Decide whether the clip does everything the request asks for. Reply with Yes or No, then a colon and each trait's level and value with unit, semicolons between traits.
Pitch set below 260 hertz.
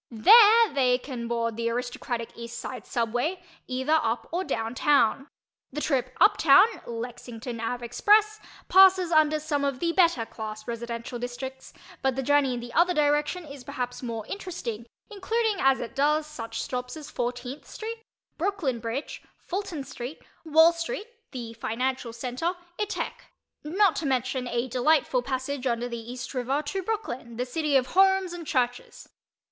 No: very high, 265 Hz